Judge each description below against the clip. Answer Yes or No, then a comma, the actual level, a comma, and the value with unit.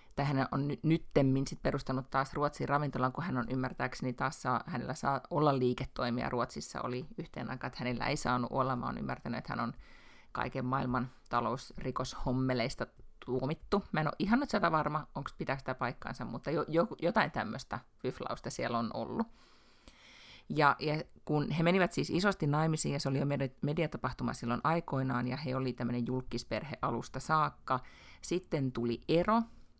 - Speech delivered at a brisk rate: Yes, fast, 165 wpm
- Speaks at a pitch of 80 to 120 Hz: No, low, 135 Hz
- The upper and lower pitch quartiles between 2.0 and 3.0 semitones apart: No, average, 3.5 semitones